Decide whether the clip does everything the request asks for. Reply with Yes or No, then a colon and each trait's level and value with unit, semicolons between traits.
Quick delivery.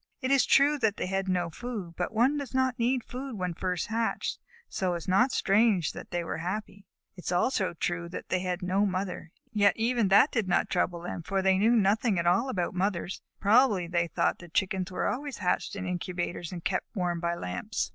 Yes: fast, 215 wpm